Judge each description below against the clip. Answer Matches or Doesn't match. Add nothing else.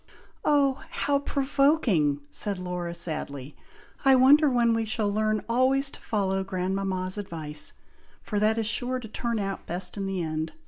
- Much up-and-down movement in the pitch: Matches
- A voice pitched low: Doesn't match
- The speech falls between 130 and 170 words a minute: Matches